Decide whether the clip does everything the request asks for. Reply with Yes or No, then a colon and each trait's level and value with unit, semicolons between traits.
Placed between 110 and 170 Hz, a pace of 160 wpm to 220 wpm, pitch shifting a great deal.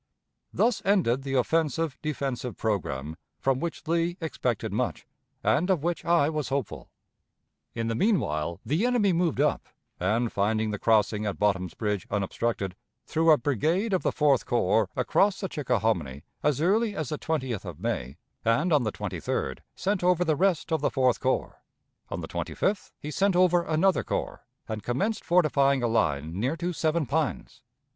Yes: medium, 140 Hz; average, 170 wpm; wide, 7.6 semitones